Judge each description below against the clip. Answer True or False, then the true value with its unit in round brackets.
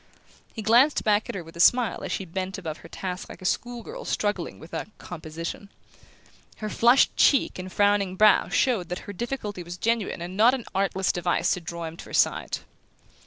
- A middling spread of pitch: True (3.7 semitones)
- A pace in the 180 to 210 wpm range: True (205 wpm)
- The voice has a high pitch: True (195 Hz)